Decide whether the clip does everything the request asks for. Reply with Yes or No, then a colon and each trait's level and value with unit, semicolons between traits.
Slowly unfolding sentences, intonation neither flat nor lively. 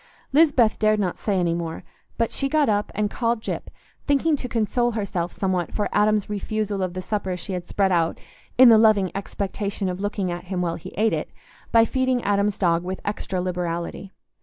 No: average, 195 wpm; average, 3.3 semitones